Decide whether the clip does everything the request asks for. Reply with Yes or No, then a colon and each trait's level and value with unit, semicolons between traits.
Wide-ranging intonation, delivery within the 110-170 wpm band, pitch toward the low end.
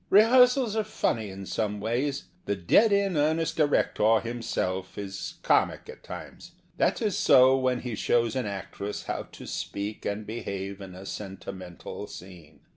Yes: wide, 6.9 semitones; average, 155 wpm; low, 110 Hz